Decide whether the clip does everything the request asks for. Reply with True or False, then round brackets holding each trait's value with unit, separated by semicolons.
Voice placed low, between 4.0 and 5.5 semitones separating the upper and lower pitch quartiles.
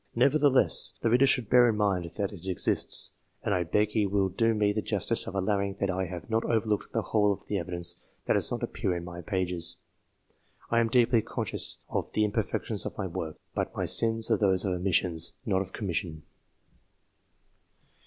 False (100 Hz; 3.6 semitones)